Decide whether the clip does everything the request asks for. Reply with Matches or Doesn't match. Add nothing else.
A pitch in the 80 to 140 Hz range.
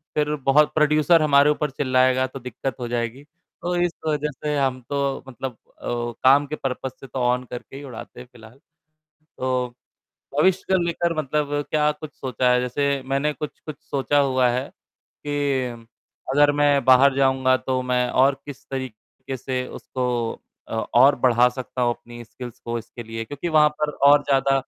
Matches